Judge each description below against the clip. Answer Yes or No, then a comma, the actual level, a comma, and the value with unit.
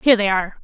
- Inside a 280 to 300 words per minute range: Yes, fast, 285 wpm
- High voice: Yes, high, 205 Hz